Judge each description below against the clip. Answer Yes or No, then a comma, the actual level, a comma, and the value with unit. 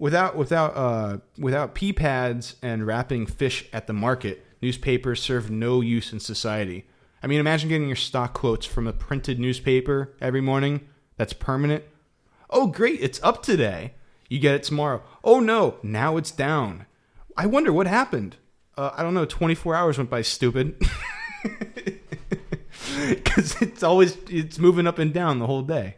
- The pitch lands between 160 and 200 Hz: No, low, 135 Hz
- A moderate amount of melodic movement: Yes, average, 4.6 semitones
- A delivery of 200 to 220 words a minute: No, average, 165 wpm